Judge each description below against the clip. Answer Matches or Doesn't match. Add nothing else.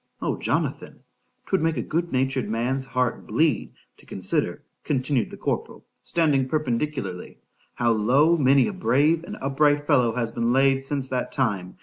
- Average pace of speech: Matches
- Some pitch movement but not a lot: Matches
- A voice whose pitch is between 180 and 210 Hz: Doesn't match